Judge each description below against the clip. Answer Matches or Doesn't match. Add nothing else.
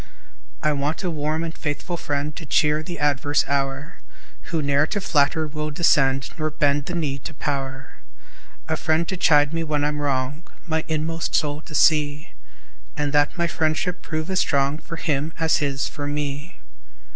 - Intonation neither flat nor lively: Doesn't match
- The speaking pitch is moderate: Matches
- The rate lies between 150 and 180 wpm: Matches